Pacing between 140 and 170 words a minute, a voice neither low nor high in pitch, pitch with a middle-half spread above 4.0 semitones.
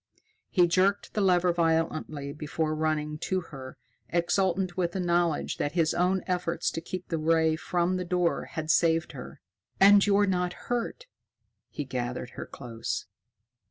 No: average, 155 wpm; medium, 170 Hz; average, 2.8 semitones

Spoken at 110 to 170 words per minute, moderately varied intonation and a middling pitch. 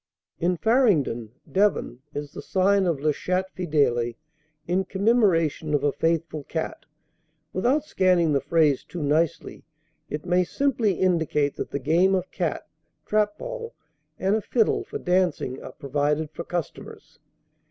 Yes: average, 140 wpm; average, 4.4 semitones; medium, 170 Hz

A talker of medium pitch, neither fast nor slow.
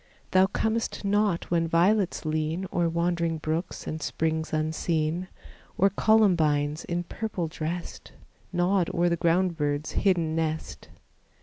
No: medium, 170 Hz; slow, 125 wpm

